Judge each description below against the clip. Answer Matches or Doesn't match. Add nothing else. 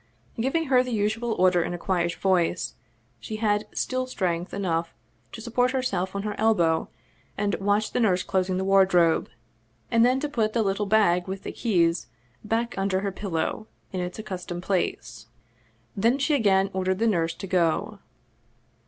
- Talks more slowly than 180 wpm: Matches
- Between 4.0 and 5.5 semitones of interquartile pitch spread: Doesn't match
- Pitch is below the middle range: Doesn't match